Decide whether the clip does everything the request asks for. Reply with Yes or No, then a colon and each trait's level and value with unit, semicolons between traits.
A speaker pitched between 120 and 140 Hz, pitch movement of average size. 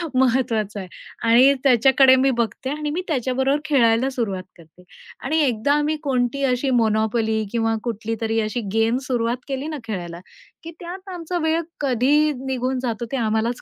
No: very high, 250 Hz; average, 3.7 semitones